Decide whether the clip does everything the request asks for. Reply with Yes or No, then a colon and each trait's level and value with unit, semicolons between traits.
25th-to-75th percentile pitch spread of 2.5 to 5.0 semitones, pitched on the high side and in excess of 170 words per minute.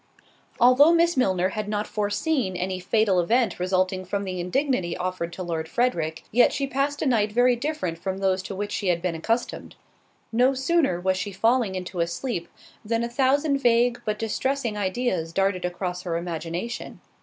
No: wide, 5.4 semitones; high, 205 Hz; average, 180 wpm